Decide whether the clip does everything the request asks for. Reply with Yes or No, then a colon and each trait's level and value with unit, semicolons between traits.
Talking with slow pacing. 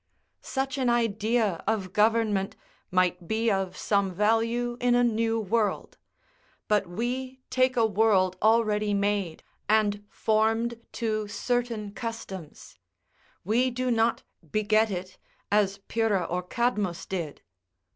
Yes: slow, 120 wpm